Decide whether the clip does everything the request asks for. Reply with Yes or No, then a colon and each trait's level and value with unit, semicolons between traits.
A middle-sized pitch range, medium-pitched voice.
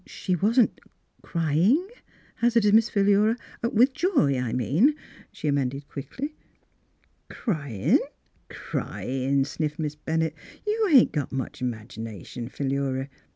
No: wide, 8.9 semitones; medium, 155 Hz